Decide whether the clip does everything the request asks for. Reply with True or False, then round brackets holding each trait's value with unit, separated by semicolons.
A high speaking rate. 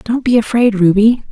False (180 wpm)